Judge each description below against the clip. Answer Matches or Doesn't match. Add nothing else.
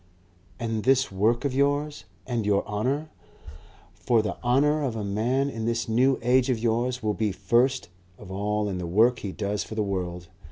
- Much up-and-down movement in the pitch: Doesn't match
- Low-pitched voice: Matches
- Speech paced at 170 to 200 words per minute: Matches